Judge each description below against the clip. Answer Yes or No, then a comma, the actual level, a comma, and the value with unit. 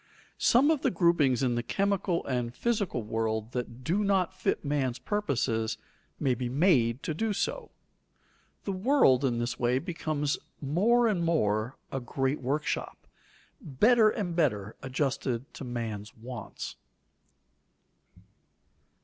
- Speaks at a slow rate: Yes, slow, 130 wpm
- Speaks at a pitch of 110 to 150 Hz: Yes, medium, 140 Hz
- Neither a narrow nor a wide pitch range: No, wide, 7.5 semitones